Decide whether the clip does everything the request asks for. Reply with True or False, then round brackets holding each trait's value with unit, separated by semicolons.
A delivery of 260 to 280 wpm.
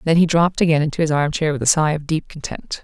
True (275 wpm)